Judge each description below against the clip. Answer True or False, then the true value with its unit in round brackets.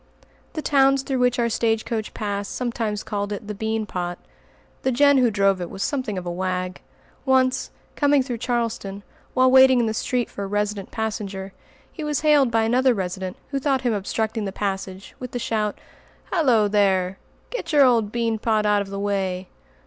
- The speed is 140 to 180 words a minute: False (190 wpm)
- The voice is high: True (220 Hz)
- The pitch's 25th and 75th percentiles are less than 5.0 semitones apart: True (4.3 semitones)